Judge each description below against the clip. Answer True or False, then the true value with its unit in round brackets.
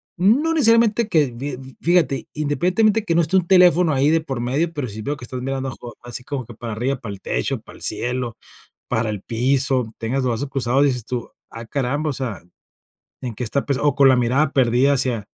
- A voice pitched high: False (135 Hz)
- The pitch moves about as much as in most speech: True (4.1 semitones)